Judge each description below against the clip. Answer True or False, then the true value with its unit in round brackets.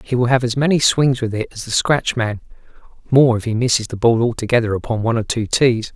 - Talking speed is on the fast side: True (240 wpm)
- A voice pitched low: True (120 Hz)